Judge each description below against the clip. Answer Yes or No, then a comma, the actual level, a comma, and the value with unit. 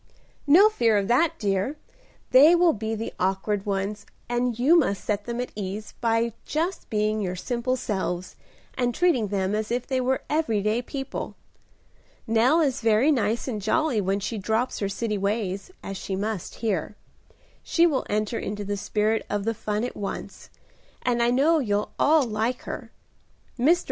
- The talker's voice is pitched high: Yes, high, 225 Hz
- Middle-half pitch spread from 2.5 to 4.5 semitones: Yes, average, 3.8 semitones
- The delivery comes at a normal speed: Yes, average, 175 wpm